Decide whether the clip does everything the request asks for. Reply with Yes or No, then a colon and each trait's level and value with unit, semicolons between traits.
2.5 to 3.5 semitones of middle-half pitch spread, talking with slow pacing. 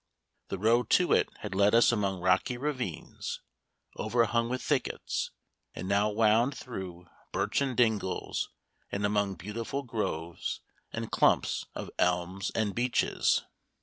No: average, 3.9 semitones; slow, 125 wpm